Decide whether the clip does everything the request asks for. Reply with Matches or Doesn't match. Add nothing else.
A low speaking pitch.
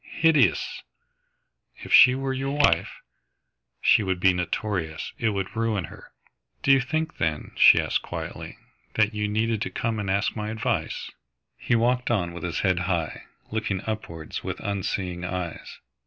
Matches